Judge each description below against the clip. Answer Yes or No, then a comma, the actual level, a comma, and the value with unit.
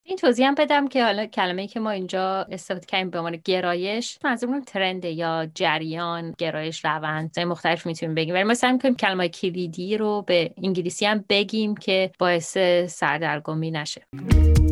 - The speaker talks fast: Yes, fast, 165 wpm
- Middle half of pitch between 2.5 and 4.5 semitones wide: Yes, average, 4.0 semitones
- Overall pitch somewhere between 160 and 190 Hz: Yes, medium, 185 Hz